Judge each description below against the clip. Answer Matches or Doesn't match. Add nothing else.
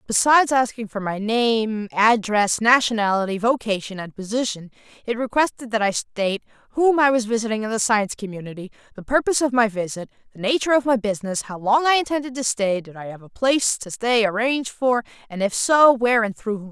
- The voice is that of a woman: Matches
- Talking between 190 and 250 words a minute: Matches